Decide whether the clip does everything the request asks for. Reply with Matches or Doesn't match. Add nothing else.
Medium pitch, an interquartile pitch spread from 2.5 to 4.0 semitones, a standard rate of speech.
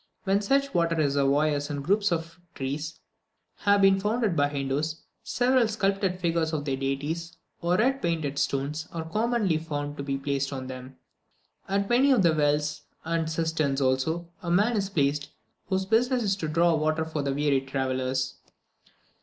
Doesn't match